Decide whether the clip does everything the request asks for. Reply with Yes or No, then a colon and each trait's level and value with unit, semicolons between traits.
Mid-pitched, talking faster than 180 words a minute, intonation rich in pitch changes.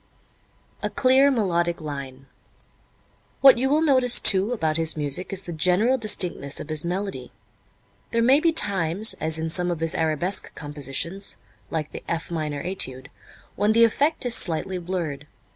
No: medium, 175 Hz; average, 160 wpm; wide, 6.1 semitones